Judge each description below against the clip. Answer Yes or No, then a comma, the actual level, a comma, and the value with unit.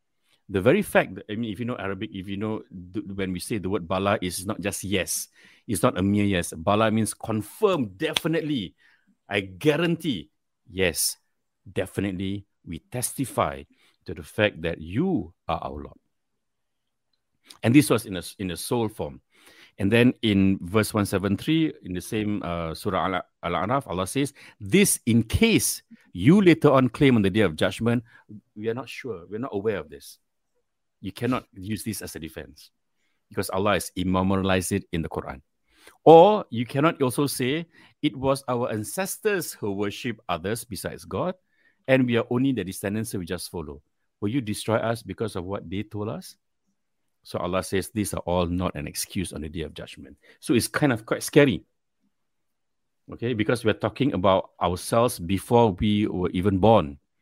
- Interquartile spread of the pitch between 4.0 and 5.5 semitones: Yes, average, 4.7 semitones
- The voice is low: Yes, low, 105 Hz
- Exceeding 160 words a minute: Yes, average, 175 wpm